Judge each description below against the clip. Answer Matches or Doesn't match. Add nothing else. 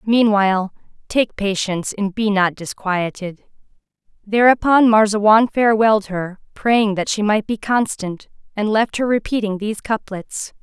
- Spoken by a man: Doesn't match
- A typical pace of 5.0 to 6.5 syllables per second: Doesn't match